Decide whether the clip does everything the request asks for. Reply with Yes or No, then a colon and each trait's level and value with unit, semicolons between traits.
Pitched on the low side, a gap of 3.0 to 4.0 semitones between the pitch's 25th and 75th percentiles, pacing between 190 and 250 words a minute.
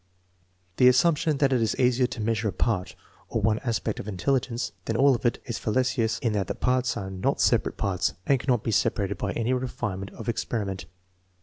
Yes: low, 115 Hz; average, 3.5 semitones; average, 200 wpm